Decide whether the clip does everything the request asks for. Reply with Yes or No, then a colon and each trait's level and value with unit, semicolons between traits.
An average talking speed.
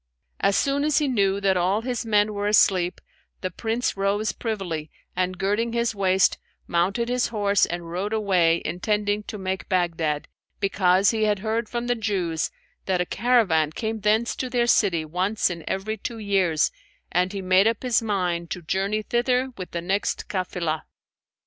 Yes: average, 175 wpm